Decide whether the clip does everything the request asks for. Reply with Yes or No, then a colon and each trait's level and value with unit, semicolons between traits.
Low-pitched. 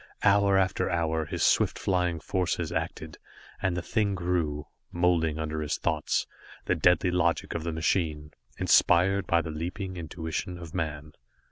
Yes: very low, 85 Hz